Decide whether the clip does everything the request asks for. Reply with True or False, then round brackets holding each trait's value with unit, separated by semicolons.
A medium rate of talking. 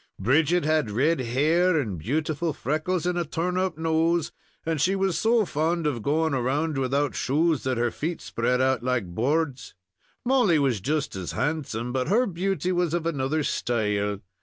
True (170 wpm)